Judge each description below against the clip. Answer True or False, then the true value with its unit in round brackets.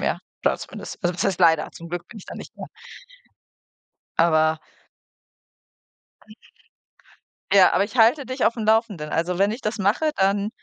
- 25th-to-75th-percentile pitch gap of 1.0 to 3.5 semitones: False (4.6 semitones)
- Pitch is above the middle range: True (195 Hz)